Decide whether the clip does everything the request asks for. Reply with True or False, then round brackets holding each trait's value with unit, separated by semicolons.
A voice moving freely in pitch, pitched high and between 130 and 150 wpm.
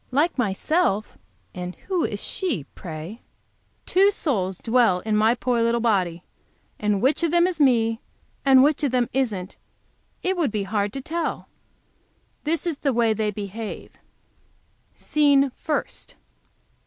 True (6.2 semitones; 235 Hz; 140 wpm)